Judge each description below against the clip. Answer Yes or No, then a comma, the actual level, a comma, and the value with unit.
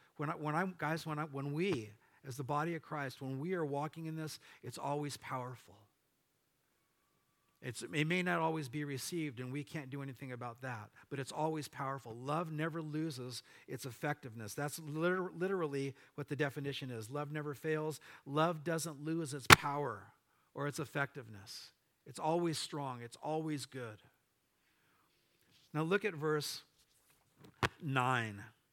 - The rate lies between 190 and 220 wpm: No, average, 155 wpm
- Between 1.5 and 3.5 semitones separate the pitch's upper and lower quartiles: Yes, average, 2.9 semitones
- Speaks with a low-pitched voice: No, medium, 145 Hz